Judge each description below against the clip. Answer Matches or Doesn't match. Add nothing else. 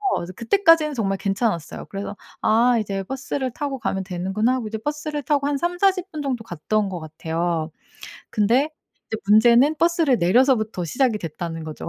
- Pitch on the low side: Doesn't match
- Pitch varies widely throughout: Matches